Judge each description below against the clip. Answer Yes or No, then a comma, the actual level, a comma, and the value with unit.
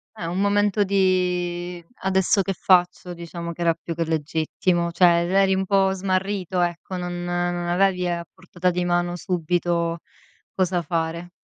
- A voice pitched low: No, medium, 175 Hz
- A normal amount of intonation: No, narrow, 1.6 semitones